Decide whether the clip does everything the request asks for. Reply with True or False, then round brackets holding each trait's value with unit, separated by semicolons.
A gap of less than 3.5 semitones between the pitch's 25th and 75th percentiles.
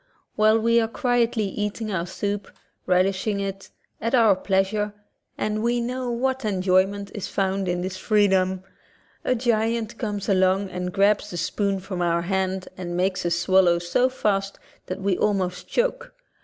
True (2.8 semitones)